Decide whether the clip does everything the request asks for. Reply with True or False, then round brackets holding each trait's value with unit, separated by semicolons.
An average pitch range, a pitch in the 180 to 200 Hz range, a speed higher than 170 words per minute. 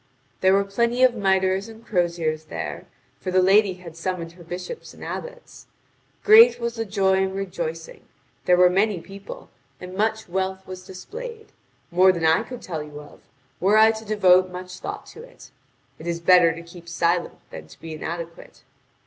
True (3.7 semitones; 185 Hz; 180 wpm)